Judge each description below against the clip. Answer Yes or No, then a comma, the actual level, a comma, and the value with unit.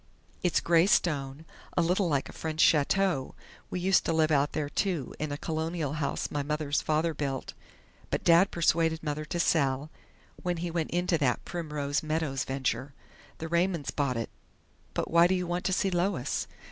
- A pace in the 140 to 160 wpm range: No, average, 180 wpm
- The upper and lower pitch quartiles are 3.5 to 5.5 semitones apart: No, average, 3.1 semitones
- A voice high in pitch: No, medium, 160 Hz